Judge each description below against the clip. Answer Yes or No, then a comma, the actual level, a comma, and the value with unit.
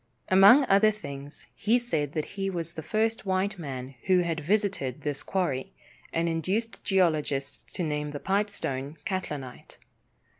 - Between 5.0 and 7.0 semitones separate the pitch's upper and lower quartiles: Yes, wide, 5.4 semitones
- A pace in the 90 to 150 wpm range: Yes, average, 145 wpm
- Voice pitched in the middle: Yes, medium, 170 Hz